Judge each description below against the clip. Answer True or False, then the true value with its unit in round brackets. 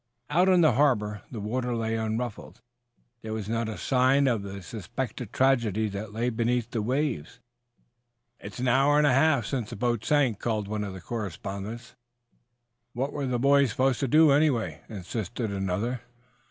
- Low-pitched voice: True (120 Hz)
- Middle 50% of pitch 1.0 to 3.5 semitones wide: False (3.9 semitones)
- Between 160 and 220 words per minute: True (170 wpm)